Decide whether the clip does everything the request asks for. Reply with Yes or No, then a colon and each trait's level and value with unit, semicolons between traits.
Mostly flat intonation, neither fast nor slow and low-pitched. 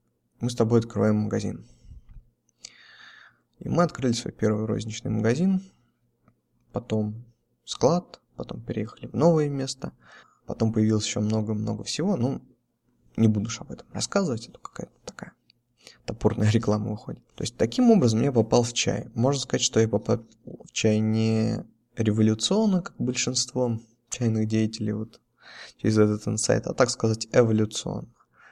Yes: narrow, 2.2 semitones; average, 140 wpm; low, 115 Hz